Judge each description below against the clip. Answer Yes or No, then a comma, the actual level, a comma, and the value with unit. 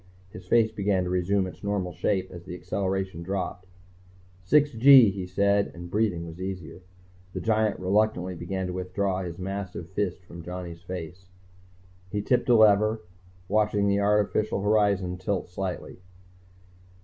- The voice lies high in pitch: No, very low, 95 Hz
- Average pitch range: No, narrow, 2.2 semitones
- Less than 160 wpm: Yes, average, 150 wpm